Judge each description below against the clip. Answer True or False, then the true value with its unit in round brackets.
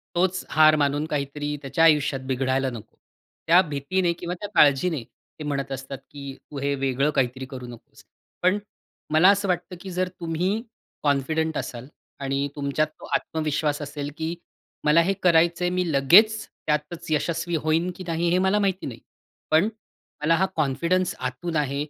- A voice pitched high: False (155 Hz)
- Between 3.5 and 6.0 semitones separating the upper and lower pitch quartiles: True (3.9 semitones)